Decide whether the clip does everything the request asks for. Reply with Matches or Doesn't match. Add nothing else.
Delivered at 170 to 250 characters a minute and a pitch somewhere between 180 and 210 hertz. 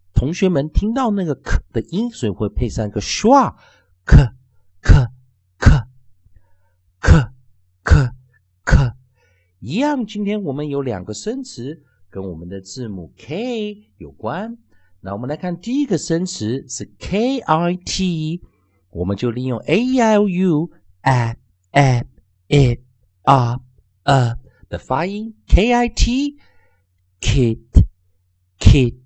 Doesn't match